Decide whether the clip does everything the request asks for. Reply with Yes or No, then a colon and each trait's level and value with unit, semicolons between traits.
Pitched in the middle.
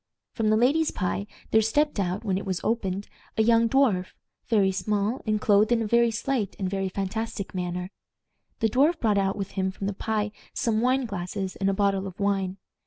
No: high, 205 Hz